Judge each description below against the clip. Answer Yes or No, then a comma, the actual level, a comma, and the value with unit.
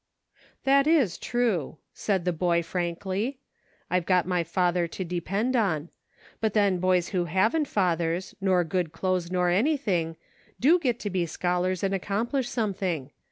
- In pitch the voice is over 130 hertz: Yes, medium, 185 Hz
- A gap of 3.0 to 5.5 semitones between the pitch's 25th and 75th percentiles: Yes, average, 3.7 semitones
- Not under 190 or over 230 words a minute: No, average, 150 wpm